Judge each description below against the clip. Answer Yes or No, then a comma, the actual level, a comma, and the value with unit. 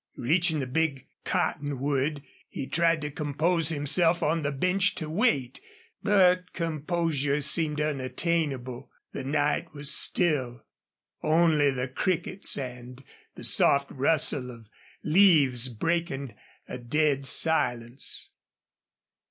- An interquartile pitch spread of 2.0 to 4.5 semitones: Yes, average, 3.8 semitones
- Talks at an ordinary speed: No, slow, 110 wpm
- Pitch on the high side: No, medium, 150 Hz